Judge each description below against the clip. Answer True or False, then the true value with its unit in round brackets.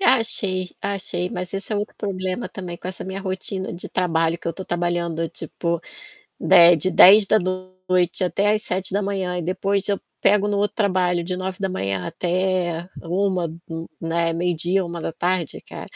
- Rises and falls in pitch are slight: True (2.1 semitones)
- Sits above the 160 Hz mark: True (185 Hz)